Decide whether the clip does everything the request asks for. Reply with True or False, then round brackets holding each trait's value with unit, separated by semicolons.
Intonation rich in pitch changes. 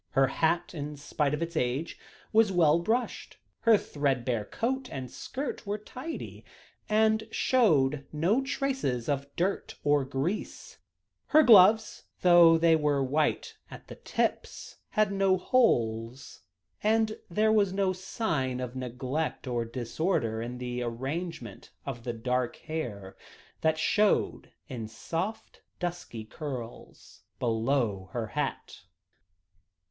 True (7.7 semitones)